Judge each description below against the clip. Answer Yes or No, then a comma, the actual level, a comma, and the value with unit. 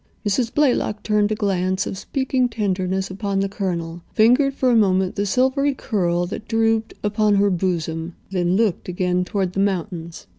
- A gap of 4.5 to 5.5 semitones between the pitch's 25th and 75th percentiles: No, average, 3.5 semitones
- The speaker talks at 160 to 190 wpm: Yes, average, 170 wpm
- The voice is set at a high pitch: Yes, high, 200 Hz